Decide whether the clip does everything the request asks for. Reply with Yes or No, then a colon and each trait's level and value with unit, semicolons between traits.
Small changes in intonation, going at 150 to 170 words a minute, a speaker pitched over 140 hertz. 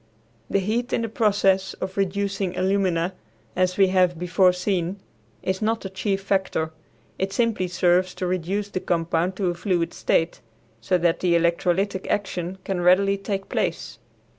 Yes: narrow, 1.8 semitones; average, 160 wpm; medium, 185 Hz